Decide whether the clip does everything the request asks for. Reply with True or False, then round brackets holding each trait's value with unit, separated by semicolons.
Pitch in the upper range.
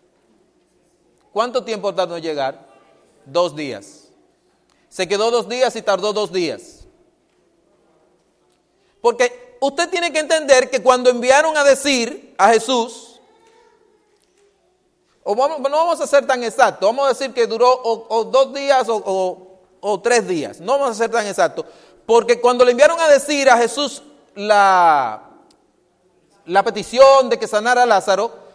True (245 Hz)